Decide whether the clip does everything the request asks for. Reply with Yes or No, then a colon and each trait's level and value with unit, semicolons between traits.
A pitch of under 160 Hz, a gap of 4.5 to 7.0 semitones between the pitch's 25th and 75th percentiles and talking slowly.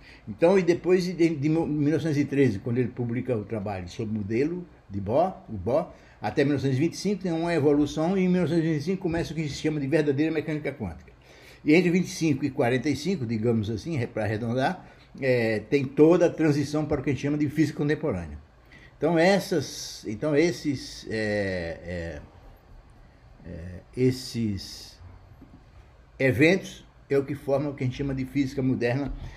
No: medium, 140 Hz; wide, 5.6 semitones; average, 160 wpm